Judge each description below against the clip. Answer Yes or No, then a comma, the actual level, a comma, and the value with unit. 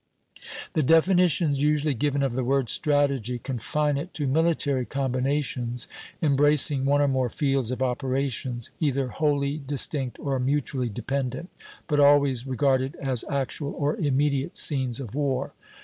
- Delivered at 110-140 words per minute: Yes, slow, 135 wpm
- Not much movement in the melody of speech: Yes, narrow, 2.0 semitones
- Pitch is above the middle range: No, medium, 140 Hz